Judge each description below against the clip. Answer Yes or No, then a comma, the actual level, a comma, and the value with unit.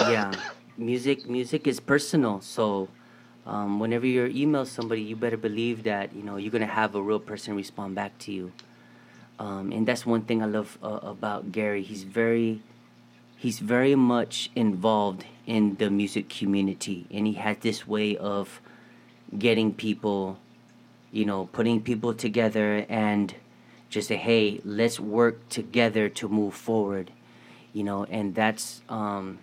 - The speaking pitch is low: Yes, low, 110 Hz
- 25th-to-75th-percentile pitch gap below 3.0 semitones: Yes, narrow, 2.5 semitones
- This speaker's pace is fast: No, average, 155 wpm